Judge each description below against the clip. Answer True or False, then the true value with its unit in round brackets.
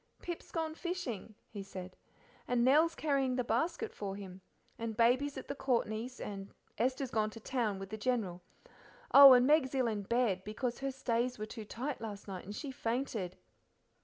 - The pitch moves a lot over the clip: False (4.2 semitones)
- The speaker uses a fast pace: False (180 wpm)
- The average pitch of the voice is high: True (240 Hz)